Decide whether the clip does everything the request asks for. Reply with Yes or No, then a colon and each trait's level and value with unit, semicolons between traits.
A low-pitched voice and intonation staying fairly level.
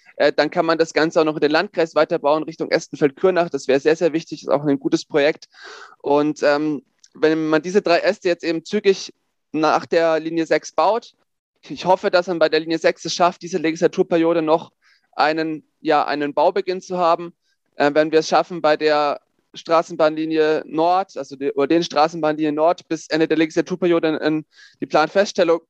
No: medium, 160 Hz; narrow, 2.1 semitones